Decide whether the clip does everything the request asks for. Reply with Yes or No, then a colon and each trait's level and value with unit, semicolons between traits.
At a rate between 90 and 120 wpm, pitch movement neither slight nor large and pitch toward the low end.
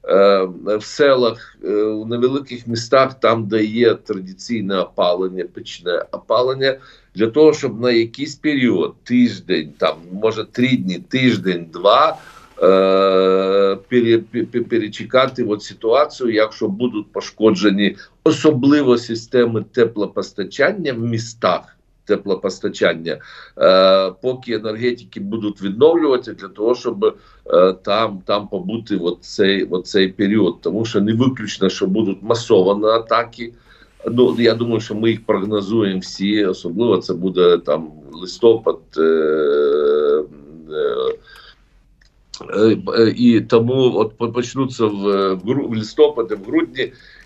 Yes: average, 110 wpm; average, 4.2 semitones; low, 115 Hz